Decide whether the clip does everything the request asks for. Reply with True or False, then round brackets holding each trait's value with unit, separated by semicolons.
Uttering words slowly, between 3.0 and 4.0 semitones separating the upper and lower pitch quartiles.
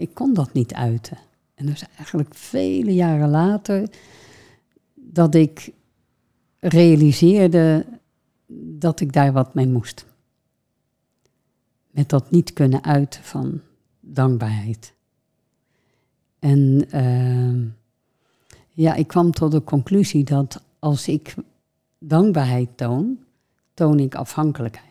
False (105 wpm; 4.6 semitones)